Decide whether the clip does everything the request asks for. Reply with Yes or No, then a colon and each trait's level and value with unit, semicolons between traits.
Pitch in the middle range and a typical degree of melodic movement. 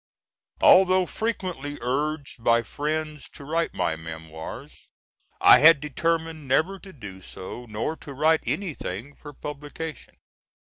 Yes: medium, 150 Hz; average, 5.0 semitones